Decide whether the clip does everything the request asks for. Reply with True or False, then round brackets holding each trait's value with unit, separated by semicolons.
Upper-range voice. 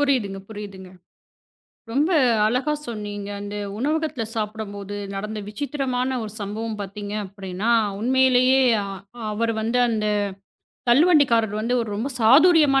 True (225 Hz)